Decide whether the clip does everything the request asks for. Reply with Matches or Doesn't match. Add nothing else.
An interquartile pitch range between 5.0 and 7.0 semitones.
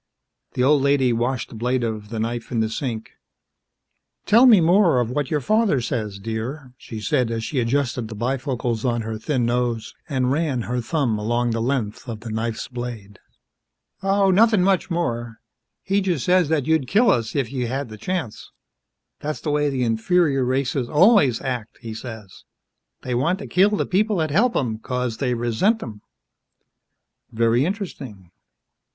Matches